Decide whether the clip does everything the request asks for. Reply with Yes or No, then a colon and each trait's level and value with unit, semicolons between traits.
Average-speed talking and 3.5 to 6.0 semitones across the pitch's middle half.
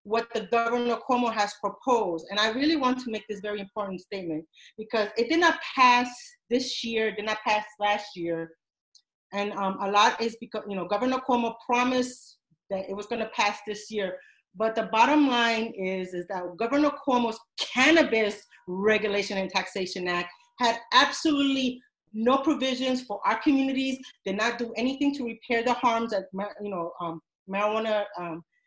Yes: average, 170 wpm; average, 3.8 semitones